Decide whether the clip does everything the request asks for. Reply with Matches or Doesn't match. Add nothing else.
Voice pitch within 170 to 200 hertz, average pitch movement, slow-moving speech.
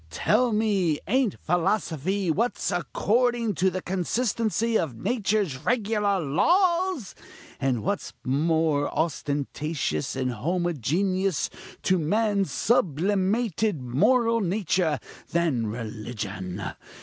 Doesn't match